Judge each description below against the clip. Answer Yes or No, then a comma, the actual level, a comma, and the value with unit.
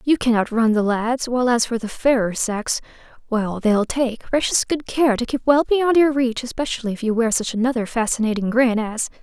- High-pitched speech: Yes, high, 240 Hz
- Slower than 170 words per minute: No, average, 195 wpm